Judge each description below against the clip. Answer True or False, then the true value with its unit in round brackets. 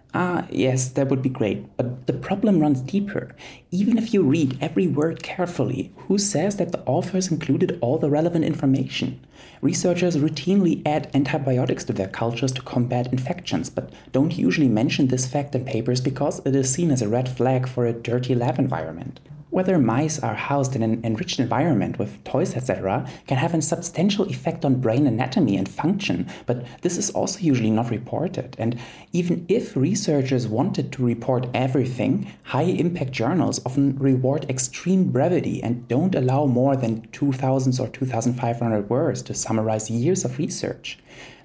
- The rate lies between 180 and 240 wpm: False (170 wpm)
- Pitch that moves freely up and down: False (4.2 semitones)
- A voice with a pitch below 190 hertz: True (135 Hz)